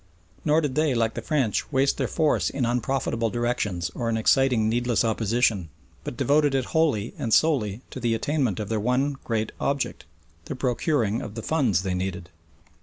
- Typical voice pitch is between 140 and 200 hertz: No, low, 120 Hz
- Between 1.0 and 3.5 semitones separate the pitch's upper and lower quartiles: No, average, 3.9 semitones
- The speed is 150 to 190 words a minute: Yes, average, 180 wpm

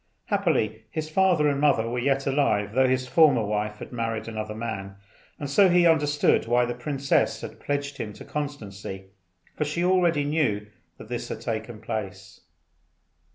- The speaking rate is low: No, average, 165 wpm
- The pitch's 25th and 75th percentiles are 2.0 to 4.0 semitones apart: No, average, 5.2 semitones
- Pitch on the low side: Yes, low, 125 Hz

